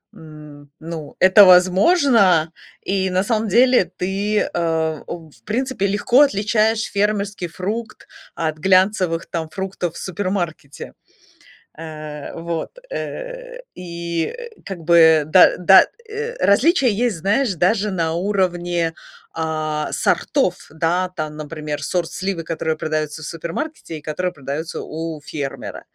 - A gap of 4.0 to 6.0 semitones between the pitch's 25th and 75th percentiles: Yes, average, 4.3 semitones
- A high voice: No, medium, 180 Hz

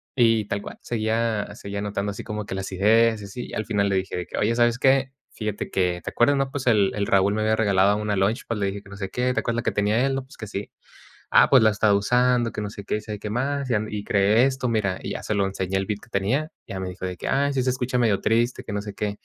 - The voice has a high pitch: No, low, 105 Hz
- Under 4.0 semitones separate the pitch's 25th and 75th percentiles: Yes, average, 2.9 semitones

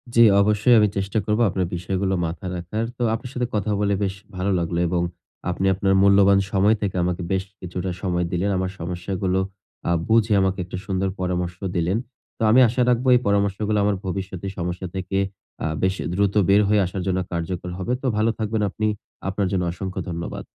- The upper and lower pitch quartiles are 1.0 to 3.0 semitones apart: Yes, narrow, 2.4 semitones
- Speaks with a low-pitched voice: Yes, very low, 95 Hz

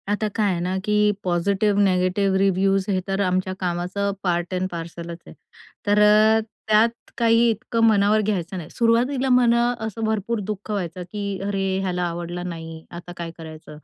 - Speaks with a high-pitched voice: Yes, high, 195 Hz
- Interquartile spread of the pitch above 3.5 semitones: No, average, 3.2 semitones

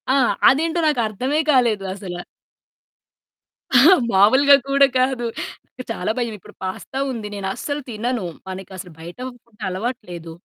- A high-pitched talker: Yes, high, 230 Hz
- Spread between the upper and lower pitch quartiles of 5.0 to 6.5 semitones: Yes, wide, 5.4 semitones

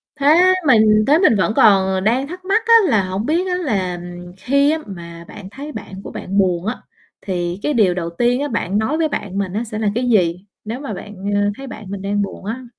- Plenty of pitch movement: Yes, wide, 6.3 semitones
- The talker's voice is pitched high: Yes, high, 215 Hz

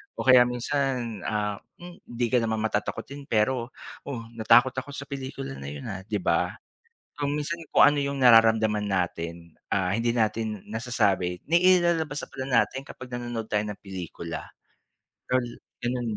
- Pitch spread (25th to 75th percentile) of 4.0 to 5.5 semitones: Yes, average, 4.3 semitones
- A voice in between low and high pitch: No, low, 115 Hz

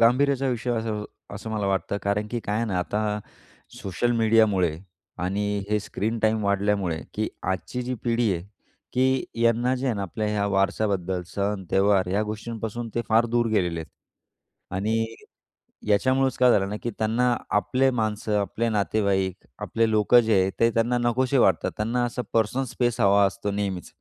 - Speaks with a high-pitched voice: No, low, 110 Hz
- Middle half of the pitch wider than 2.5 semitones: Yes, average, 2.9 semitones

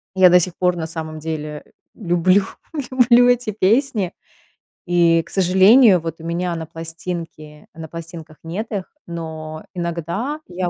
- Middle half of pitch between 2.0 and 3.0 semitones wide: Yes, average, 2.7 semitones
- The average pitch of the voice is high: No, medium, 175 Hz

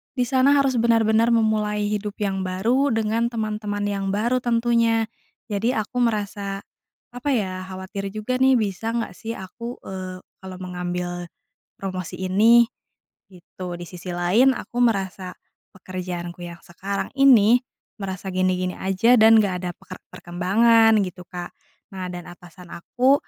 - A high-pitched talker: Yes, high, 205 Hz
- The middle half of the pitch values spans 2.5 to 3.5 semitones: No, average, 3.9 semitones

